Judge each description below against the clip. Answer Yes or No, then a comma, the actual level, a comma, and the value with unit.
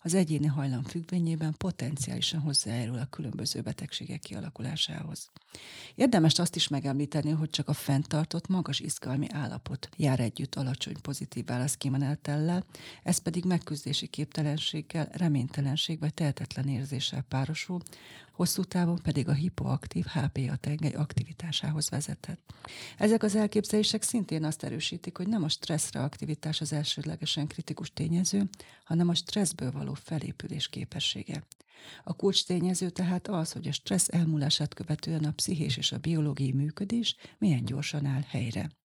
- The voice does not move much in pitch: No, average, 3.3 semitones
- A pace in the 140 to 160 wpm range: No, average, 130 wpm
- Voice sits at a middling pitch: Yes, medium, 155 Hz